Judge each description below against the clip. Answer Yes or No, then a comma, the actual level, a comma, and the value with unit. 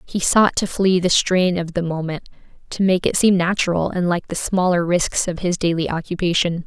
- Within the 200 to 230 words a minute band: Yes, fast, 205 wpm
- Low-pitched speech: No, medium, 175 Hz